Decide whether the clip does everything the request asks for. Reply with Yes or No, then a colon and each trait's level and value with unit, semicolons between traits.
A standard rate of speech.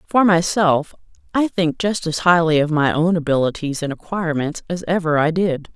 Yes: average, 175 wpm